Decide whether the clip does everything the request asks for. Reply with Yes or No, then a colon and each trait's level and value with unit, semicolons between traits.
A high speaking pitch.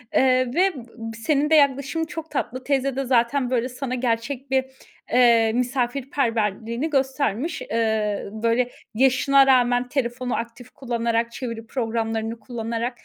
Yes: high, 245 Hz